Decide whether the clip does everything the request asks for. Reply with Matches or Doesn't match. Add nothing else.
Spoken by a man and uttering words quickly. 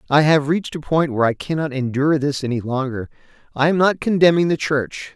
Matches